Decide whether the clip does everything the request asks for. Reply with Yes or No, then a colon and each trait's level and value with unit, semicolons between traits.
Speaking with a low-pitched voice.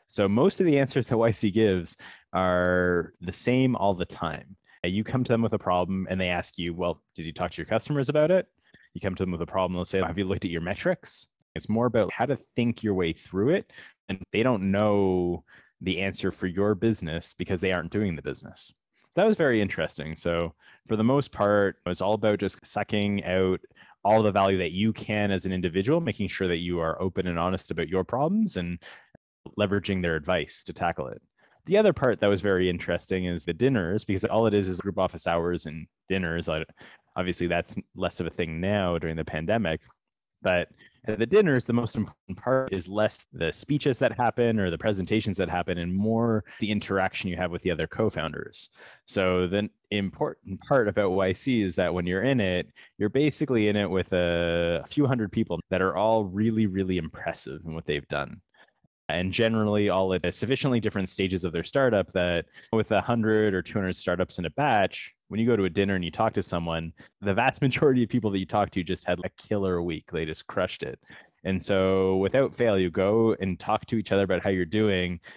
Yes: very low, 95 Hz